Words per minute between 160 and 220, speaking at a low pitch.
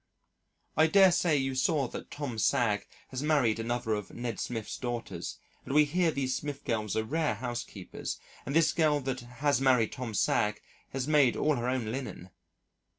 Yes: average, 175 wpm; low, 130 Hz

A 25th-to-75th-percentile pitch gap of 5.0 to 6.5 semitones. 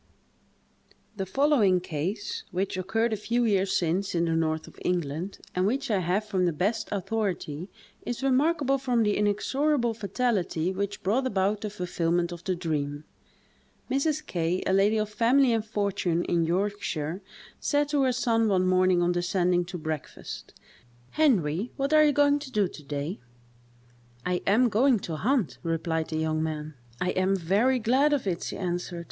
Yes: average, 5.3 semitones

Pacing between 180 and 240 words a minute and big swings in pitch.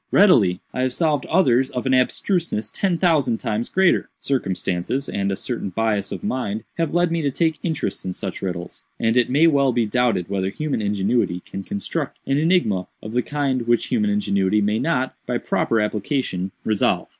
Yes: average, 185 wpm; wide, 6.8 semitones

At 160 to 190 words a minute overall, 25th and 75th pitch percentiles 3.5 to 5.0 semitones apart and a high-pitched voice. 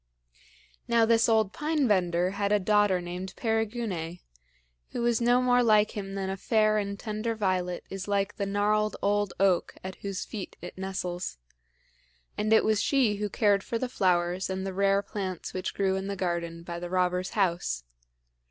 No: average, 180 wpm; narrow, 2.6 semitones; high, 200 Hz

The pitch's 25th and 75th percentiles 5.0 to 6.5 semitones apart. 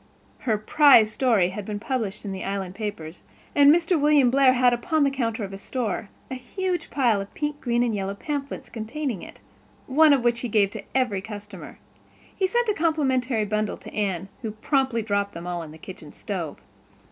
Yes: wide, 5.4 semitones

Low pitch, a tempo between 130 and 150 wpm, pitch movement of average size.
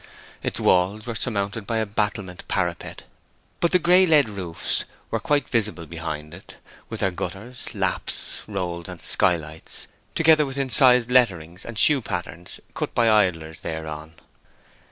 No: low, 100 Hz; average, 145 wpm; wide, 6.2 semitones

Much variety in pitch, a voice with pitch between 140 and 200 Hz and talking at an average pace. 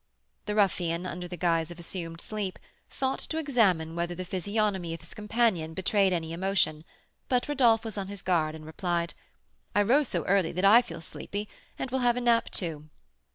No: average, 4.4 semitones; medium, 185 Hz; average, 190 wpm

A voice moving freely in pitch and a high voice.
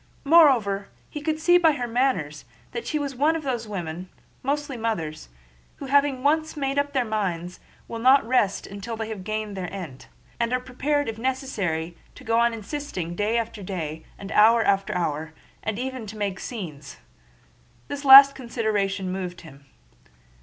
Yes: wide, 6.5 semitones; high, 225 Hz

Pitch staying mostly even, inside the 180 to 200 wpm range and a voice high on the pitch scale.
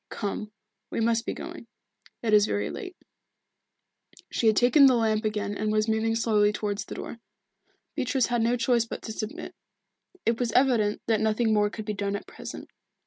Yes: narrow, 2.0 semitones; average, 185 wpm; high, 220 Hz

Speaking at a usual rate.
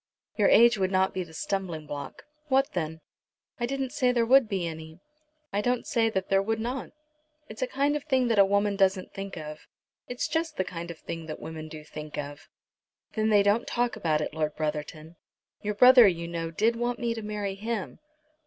No: fast, 210 wpm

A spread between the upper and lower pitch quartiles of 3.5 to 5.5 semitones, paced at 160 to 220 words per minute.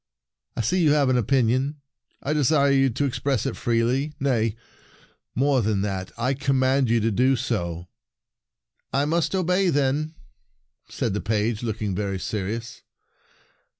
No: average, 4.2 semitones; average, 150 wpm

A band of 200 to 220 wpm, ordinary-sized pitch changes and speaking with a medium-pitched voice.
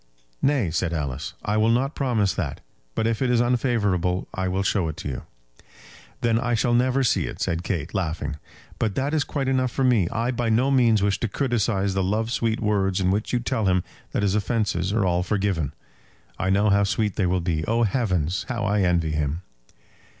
No: fast, 205 wpm; average, 4.5 semitones; low, 105 Hz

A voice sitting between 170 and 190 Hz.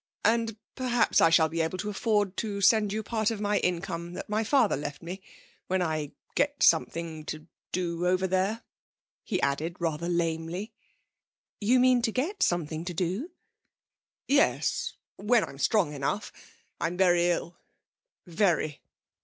Yes: medium, 185 Hz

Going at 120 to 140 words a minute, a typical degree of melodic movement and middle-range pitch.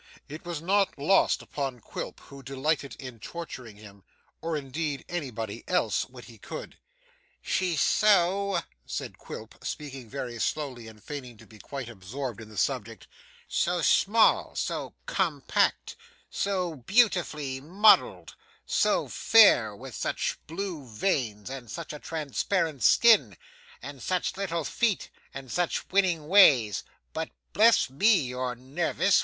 No: slow, 135 wpm; wide, 6.5 semitones; medium, 145 Hz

